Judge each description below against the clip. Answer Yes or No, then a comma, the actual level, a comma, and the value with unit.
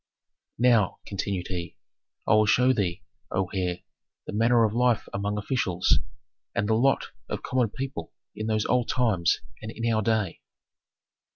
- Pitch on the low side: Yes, low, 110 Hz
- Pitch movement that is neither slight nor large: Yes, average, 3.3 semitones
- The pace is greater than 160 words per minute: No, average, 155 wpm